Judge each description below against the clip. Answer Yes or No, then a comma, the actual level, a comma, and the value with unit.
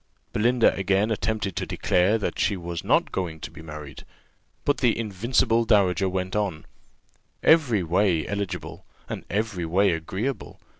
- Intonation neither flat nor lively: Yes, average, 3.8 semitones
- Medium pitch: No, low, 100 Hz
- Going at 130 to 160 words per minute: Yes, average, 145 wpm